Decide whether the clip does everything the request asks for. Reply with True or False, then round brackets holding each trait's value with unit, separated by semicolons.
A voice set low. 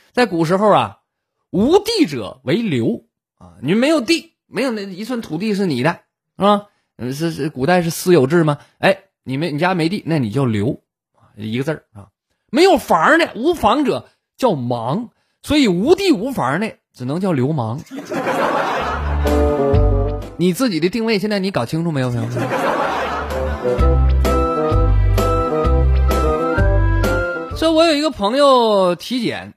False (165 Hz)